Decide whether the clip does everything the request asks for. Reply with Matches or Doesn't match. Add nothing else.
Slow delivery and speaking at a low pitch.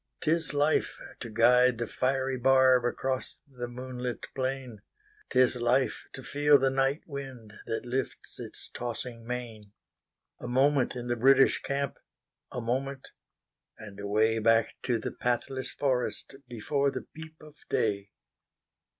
Matches